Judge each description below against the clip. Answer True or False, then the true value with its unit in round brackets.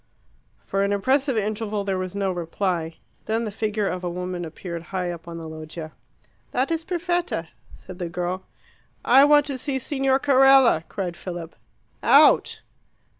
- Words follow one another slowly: False (160 wpm)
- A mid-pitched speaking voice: False (195 Hz)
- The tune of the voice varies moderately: False (7.1 semitones)